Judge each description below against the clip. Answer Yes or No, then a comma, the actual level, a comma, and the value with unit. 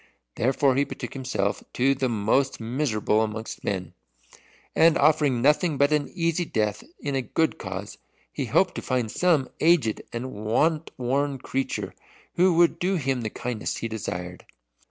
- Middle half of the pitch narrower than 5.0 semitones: No, average, 5.3 semitones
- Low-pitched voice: Yes, low, 130 Hz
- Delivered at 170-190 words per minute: No, average, 155 wpm